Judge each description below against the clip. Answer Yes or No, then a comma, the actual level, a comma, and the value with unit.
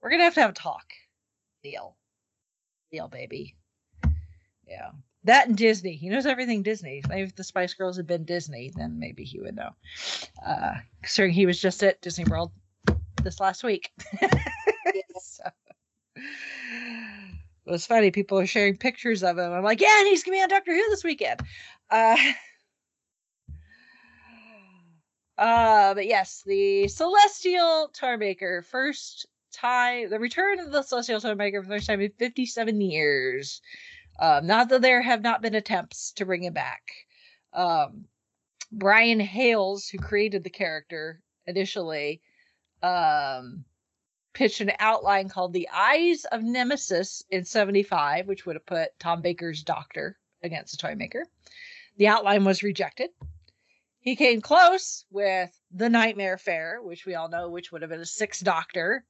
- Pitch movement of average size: No, wide, 6.0 semitones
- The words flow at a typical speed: Yes, average, 155 wpm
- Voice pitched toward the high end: Yes, high, 205 Hz